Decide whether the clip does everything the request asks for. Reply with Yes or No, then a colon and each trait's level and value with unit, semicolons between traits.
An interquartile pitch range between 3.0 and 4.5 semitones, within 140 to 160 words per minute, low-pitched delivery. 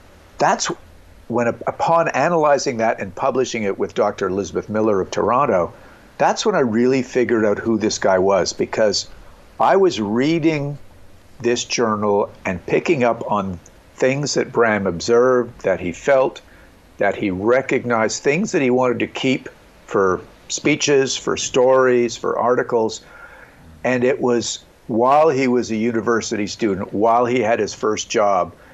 Yes: average, 3.6 semitones; average, 150 wpm; low, 120 Hz